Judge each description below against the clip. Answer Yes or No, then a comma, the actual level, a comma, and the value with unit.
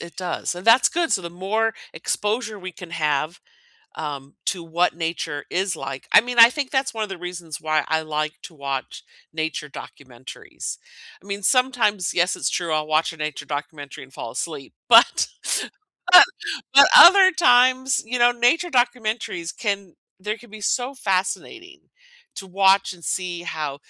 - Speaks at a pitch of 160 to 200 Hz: Yes, medium, 185 Hz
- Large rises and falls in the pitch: Yes, wide, 6.9 semitones